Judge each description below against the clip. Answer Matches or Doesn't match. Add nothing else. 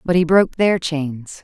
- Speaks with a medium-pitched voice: Matches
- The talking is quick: Matches